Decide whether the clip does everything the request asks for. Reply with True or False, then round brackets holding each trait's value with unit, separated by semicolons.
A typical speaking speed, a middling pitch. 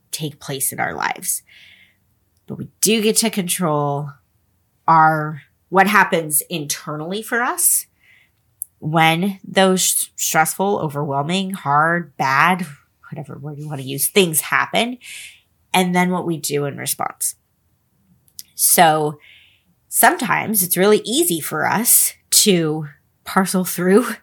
False (120 wpm; 160 Hz)